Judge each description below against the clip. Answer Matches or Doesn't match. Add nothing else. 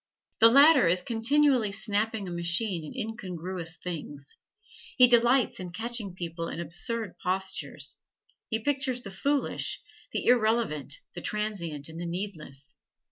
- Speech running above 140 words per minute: Doesn't match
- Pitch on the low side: Doesn't match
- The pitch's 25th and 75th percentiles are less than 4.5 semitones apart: Doesn't match